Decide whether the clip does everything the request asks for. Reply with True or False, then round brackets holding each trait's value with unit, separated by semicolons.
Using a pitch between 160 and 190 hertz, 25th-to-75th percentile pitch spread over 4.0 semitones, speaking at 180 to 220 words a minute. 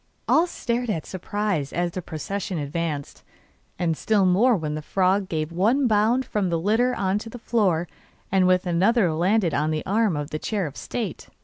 True (185 Hz; 4.6 semitones; 190 wpm)